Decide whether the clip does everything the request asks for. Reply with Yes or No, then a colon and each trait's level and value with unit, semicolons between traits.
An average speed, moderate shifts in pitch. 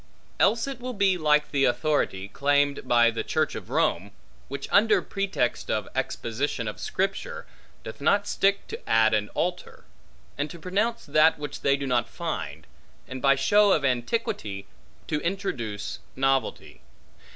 No: average, 150 wpm; wide, 7.6 semitones